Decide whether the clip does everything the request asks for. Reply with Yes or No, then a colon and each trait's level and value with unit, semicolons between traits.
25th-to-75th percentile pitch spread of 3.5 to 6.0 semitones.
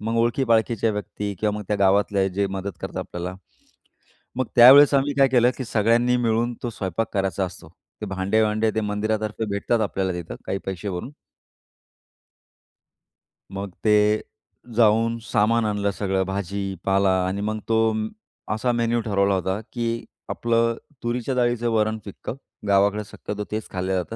No: average, 2.8 semitones